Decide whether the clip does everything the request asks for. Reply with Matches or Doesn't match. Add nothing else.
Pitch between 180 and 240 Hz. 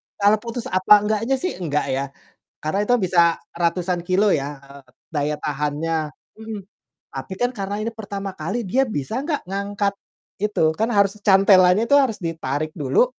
Matches